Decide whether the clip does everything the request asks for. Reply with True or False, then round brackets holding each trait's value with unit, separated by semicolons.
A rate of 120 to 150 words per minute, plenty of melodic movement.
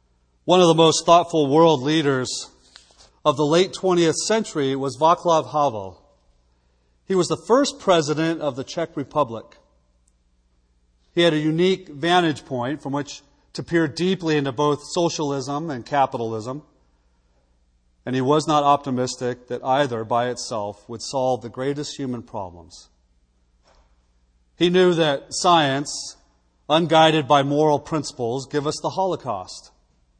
True (135 wpm; 7.7 semitones)